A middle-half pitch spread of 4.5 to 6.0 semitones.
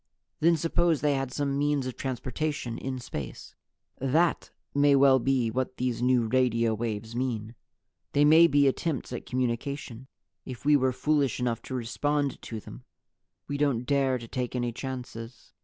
No: average, 3.0 semitones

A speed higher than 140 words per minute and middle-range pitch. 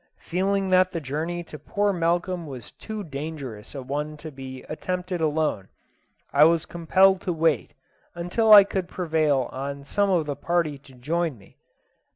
Yes: average, 165 wpm; medium, 160 Hz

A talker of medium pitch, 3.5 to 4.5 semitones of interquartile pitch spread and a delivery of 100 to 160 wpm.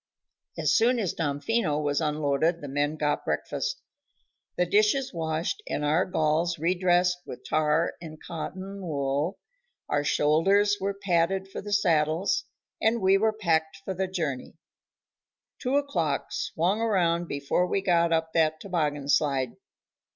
Yes: medium, 170 Hz; average, 4.2 semitones; average, 140 wpm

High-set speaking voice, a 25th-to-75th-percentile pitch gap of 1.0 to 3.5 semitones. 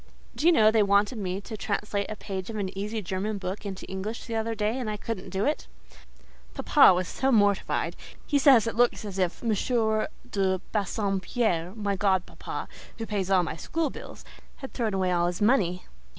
Yes: high, 205 Hz; average, 3.0 semitones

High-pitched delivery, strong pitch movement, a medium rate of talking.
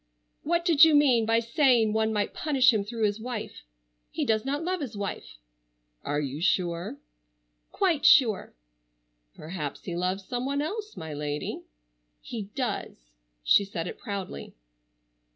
Yes: high, 220 Hz; wide, 7.2 semitones; average, 150 wpm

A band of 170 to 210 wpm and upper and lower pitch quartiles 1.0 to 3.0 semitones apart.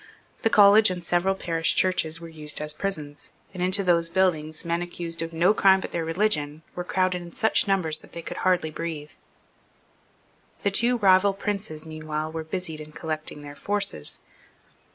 No: average, 175 wpm; average, 3.4 semitones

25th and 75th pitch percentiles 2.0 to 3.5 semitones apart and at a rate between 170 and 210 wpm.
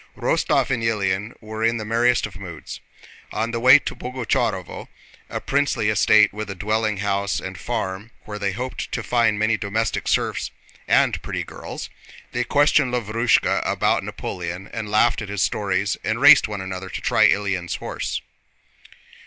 No: average, 2.8 semitones; average, 160 wpm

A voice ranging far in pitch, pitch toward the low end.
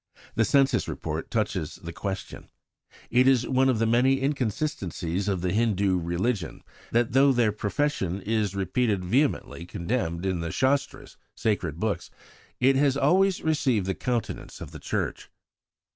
Yes: wide, 6.0 semitones; low, 110 Hz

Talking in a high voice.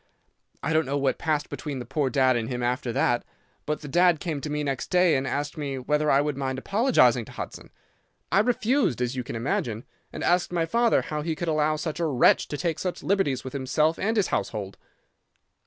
No: medium, 150 Hz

